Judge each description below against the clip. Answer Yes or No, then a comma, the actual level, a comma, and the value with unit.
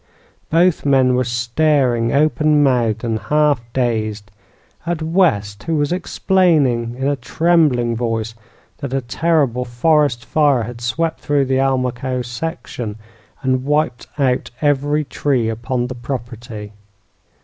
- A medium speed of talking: No, slow, 125 wpm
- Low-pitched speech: Yes, low, 130 Hz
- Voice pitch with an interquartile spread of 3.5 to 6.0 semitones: Yes, average, 4.0 semitones